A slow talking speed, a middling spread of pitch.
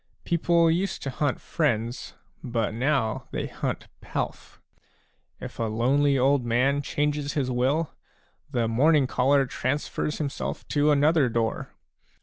Yes: slow, 130 wpm; average, 3.4 semitones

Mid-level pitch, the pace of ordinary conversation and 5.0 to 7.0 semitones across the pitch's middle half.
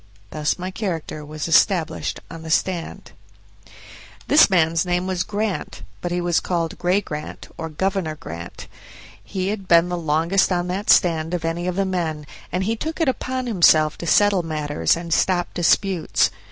No: medium, 175 Hz; average, 170 wpm; average, 2.8 semitones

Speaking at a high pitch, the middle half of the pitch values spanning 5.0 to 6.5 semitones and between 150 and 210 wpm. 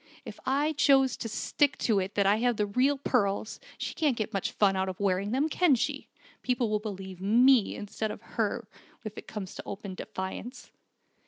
No: high, 215 Hz; average, 4.6 semitones; average, 195 wpm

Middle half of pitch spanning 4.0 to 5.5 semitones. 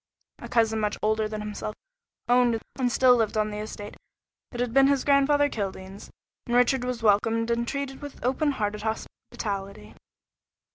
No: average, 3.1 semitones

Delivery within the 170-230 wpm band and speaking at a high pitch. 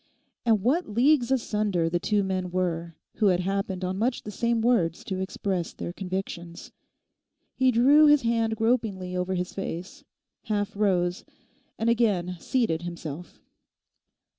No: average, 140 wpm; high, 195 Hz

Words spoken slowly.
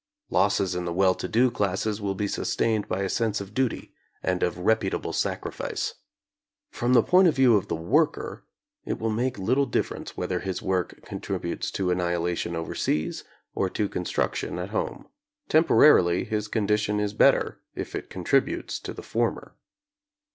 No: average, 165 wpm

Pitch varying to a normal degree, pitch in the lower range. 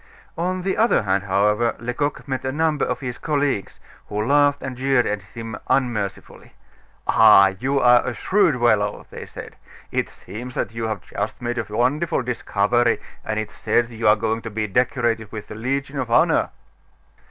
Yes: average, 3.9 semitones; low, 120 Hz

